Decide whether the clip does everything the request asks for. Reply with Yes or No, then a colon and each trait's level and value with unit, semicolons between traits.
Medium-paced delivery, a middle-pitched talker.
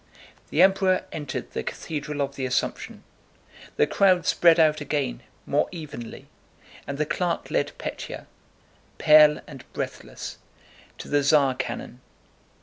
No: slow, 120 wpm; medium, 150 Hz